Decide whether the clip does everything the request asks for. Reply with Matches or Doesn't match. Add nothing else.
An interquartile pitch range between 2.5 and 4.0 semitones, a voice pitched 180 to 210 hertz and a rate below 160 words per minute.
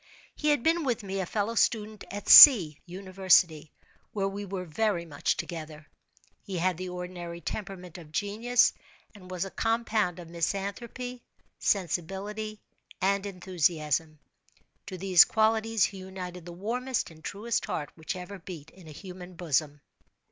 Matches